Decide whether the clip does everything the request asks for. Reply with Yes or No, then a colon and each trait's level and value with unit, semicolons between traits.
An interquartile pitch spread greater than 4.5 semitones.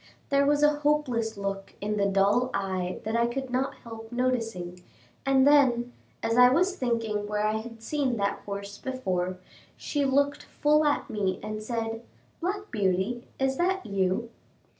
Yes: average, 5.0 semitones